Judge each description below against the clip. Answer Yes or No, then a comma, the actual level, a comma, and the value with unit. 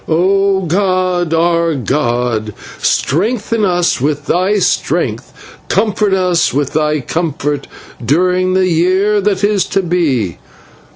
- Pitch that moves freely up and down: No, average, 4.2 semitones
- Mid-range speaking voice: Yes, medium, 175 Hz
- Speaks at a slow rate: Yes, slow, 115 wpm